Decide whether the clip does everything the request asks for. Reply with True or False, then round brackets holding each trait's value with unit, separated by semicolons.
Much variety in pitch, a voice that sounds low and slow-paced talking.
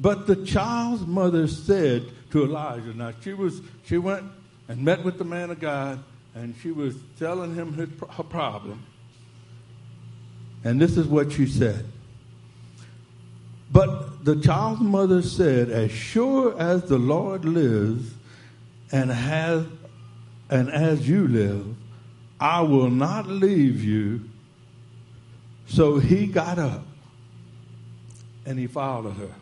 True (5.9 semitones; 130 Hz; 130 wpm)